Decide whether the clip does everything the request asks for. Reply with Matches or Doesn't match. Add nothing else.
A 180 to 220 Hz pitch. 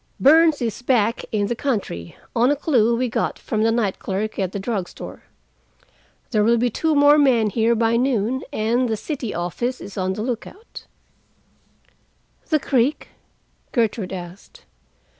Doesn't match